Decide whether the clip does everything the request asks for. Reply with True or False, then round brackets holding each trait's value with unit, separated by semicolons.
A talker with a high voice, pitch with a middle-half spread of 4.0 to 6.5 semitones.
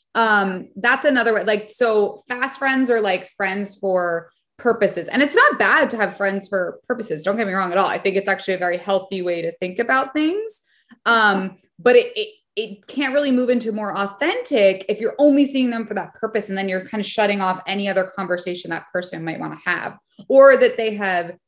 True (205 Hz; 4.7 semitones)